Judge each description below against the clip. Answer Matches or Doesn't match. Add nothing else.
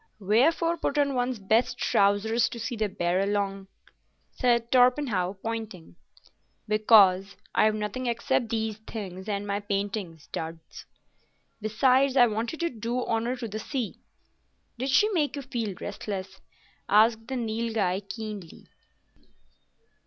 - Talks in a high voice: Matches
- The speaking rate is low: Matches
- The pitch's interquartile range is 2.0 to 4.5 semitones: Matches